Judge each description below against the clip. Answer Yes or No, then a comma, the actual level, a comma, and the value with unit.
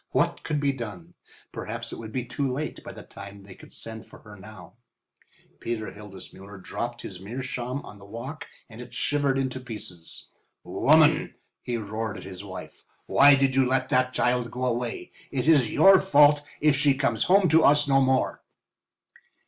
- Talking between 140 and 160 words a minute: No, average, 180 wpm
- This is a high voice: No, low, 125 Hz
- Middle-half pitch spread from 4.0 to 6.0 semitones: Yes, average, 4.3 semitones